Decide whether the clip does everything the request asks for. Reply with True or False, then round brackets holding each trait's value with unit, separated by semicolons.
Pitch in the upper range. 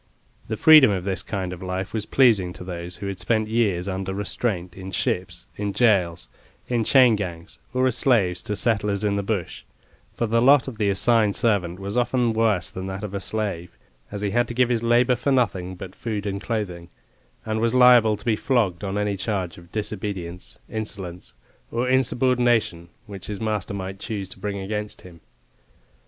False (105 Hz)